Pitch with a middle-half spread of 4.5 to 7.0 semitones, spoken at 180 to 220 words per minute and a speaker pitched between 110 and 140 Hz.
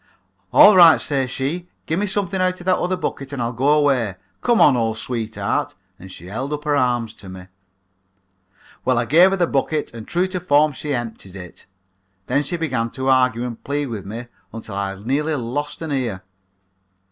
Yes: average, 5.3 semitones; average, 195 wpm; low, 135 Hz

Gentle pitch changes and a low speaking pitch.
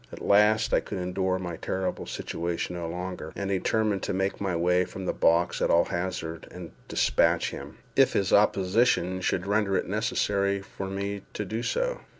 Yes: narrow, 2.1 semitones; very low, 95 Hz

